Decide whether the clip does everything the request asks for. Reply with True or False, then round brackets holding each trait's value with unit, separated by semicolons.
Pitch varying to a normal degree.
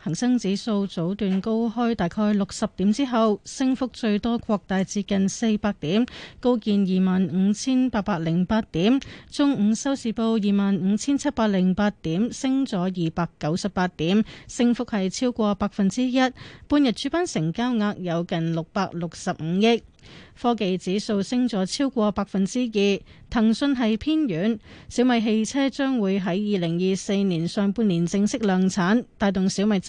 True (3.8 semitones)